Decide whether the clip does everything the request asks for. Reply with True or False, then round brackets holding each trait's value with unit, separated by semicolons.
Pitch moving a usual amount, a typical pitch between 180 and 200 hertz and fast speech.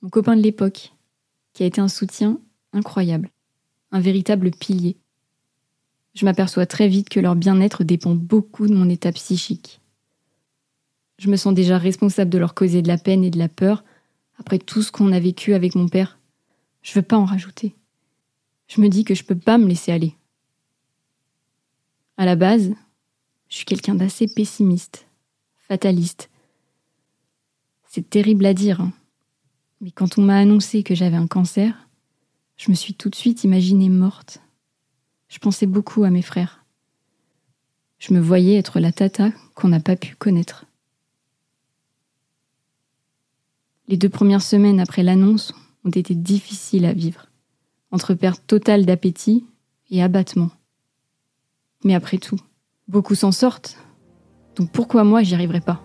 False (4.2 semitones; 185 Hz; 155 wpm)